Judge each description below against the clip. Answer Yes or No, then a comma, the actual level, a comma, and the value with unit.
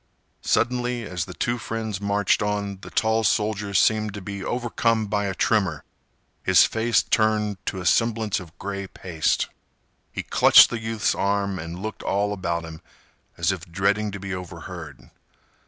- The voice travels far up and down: No, average, 2.8 semitones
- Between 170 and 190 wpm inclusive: No, average, 160 wpm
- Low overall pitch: Yes, low, 100 Hz